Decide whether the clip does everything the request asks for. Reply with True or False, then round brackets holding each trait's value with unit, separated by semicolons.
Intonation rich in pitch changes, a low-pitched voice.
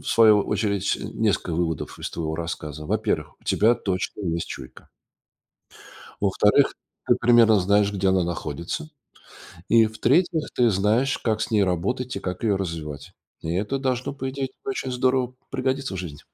True (6.1 semitones; 105 Hz)